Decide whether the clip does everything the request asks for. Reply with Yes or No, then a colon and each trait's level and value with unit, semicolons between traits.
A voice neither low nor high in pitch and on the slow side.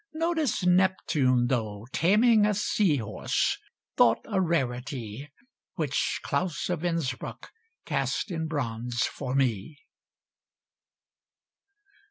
Yes: medium, 150 Hz; slow, 95 wpm